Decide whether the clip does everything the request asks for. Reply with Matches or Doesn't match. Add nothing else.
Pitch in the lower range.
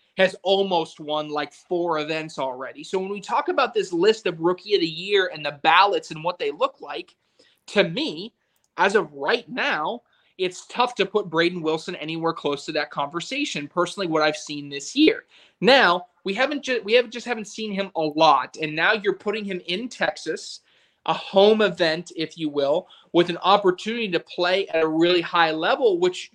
Doesn't match